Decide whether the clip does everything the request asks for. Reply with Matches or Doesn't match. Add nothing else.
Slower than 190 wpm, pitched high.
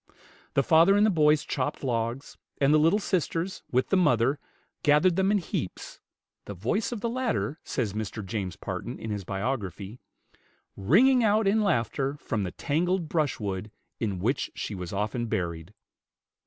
Doesn't match